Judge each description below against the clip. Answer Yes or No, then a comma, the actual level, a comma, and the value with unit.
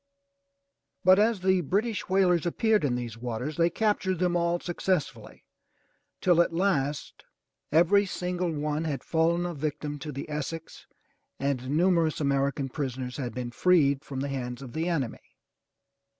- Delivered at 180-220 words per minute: No, average, 150 wpm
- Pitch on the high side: No, medium, 160 Hz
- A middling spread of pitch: Yes, average, 4.5 semitones